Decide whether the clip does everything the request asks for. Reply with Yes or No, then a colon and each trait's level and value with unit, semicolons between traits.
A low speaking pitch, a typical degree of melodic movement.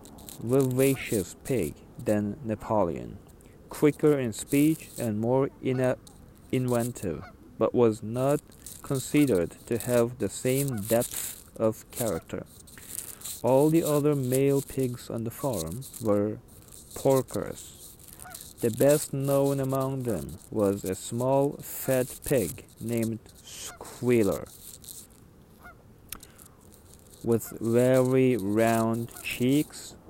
Yes: low, 120 Hz; average, 4.0 semitones